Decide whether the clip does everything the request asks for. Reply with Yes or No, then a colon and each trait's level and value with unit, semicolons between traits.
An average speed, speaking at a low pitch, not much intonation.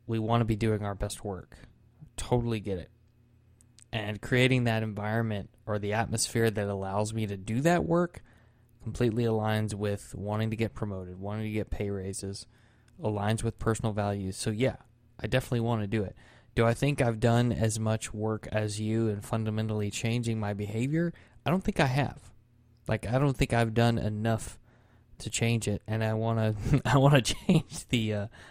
Yes: average, 185 wpm; low, 110 Hz; narrow, 1.9 semitones